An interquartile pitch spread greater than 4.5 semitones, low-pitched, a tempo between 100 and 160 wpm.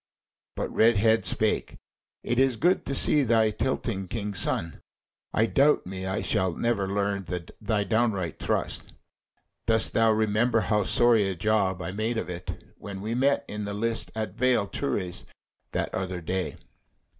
No: average, 3.2 semitones; low, 110 Hz; average, 155 wpm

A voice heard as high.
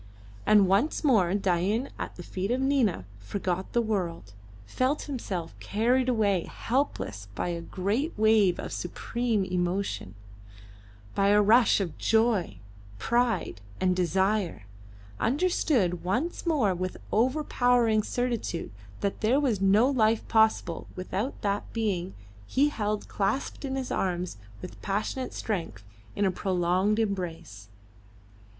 Yes: high, 205 Hz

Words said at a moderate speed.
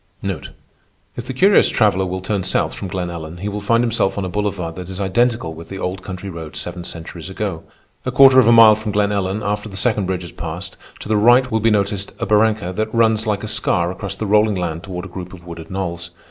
No: fast, 240 wpm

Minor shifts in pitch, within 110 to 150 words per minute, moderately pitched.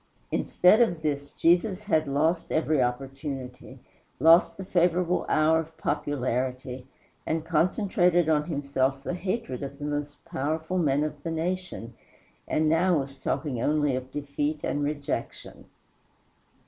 No: average, 3.3 semitones; slow, 135 wpm; medium, 150 Hz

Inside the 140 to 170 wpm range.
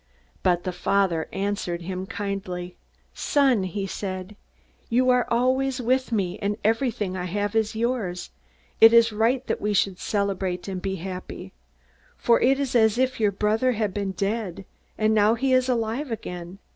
Yes: average, 165 wpm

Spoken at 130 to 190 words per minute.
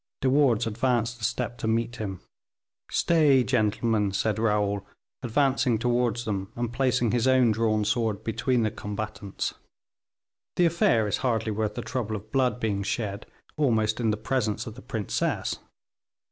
Yes: average, 155 wpm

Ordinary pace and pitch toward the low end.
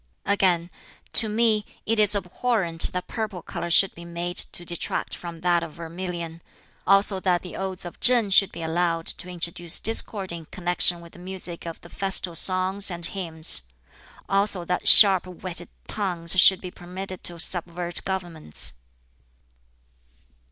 No: average, 150 wpm; medium, 180 Hz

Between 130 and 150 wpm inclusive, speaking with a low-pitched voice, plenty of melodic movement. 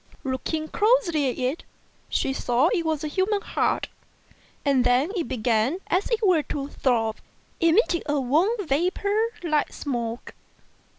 No: average, 140 wpm; very high, 300 Hz; wide, 5.7 semitones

